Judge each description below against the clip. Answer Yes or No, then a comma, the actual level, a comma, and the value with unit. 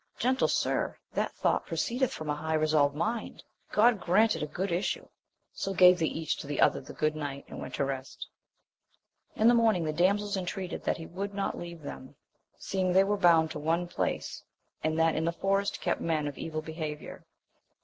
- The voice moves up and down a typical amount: Yes, average, 4.2 semitones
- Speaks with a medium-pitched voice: Yes, medium, 170 Hz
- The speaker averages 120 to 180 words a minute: No, average, 195 wpm